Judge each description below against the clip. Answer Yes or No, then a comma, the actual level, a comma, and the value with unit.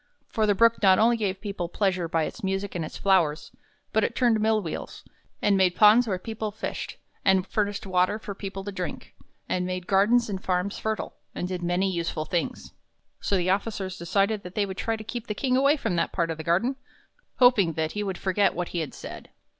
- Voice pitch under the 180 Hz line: No, high, 195 Hz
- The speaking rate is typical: No, fast, 215 wpm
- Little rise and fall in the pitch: No, average, 3.2 semitones